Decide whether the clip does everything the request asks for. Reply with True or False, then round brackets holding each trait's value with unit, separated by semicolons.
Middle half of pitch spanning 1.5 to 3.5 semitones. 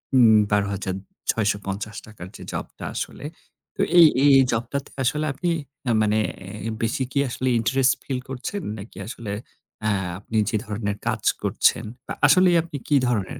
False (4.7 semitones)